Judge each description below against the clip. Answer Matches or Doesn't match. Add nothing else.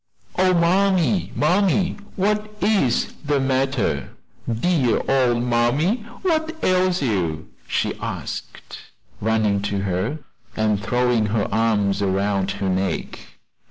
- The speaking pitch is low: Matches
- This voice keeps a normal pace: Doesn't match